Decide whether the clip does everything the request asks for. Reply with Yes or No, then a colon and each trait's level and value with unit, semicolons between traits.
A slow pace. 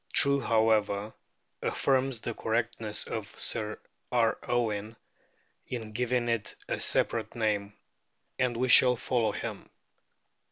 Yes: slow, 115 wpm